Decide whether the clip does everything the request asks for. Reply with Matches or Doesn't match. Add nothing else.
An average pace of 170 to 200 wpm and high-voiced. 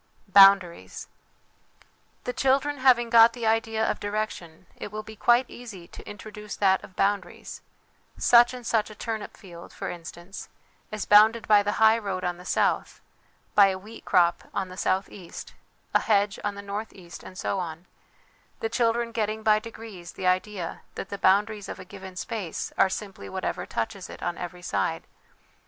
Matches